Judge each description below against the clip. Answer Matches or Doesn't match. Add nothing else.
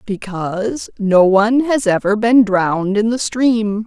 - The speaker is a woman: Matches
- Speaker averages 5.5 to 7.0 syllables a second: Doesn't match